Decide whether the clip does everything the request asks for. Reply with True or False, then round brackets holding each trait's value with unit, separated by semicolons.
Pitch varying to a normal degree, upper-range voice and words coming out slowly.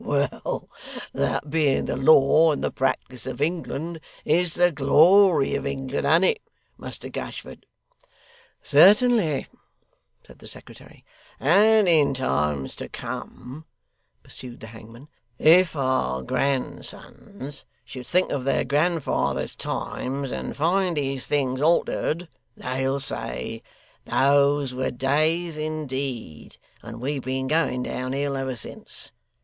False (3.6 semitones; 140 Hz; 120 wpm)